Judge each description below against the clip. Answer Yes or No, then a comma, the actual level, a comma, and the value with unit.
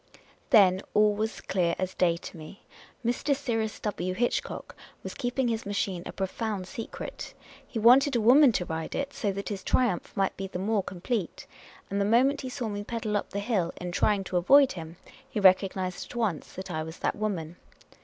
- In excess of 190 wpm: Yes, fast, 205 wpm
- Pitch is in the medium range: No, high, 205 Hz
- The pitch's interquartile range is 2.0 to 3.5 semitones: No, average, 4.1 semitones